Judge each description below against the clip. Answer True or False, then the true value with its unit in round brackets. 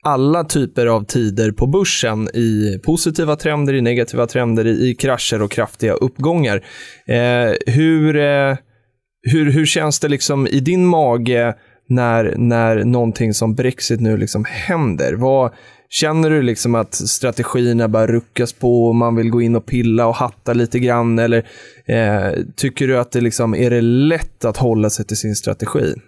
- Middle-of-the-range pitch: False (120 Hz)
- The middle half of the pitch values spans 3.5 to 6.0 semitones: False (3.0 semitones)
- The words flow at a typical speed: True (165 wpm)